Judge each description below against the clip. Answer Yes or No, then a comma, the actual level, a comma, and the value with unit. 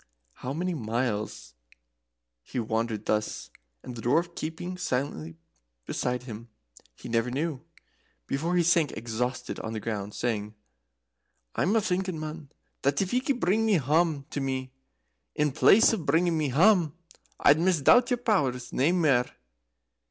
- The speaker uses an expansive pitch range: Yes, wide, 6.3 semitones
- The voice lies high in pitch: No, medium, 140 Hz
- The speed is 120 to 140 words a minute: Yes, slow, 135 wpm